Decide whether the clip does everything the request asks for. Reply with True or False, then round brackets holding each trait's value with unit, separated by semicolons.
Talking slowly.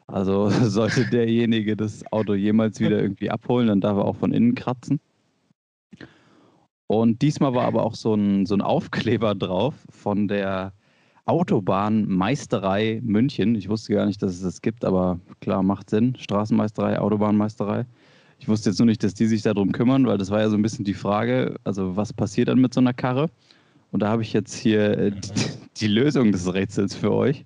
False (185 wpm)